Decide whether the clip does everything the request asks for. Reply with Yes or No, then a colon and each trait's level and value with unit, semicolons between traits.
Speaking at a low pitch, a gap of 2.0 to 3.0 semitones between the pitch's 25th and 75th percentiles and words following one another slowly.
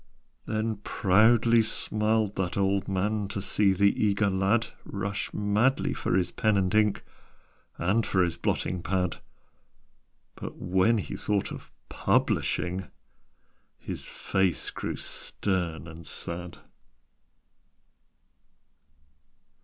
Yes: low, 100 Hz; narrow, 2.6 semitones; slow, 105 wpm